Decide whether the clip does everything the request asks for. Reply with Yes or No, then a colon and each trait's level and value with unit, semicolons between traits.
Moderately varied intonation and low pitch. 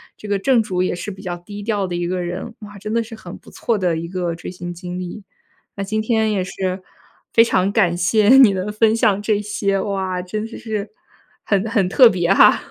No: average, 3.0 semitones; high, 195 Hz